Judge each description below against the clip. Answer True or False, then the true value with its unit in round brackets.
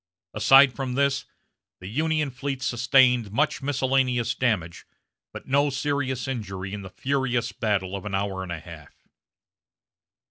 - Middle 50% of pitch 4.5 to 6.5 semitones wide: True (5.3 semitones)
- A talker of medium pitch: False (125 Hz)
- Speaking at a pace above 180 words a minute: False (140 wpm)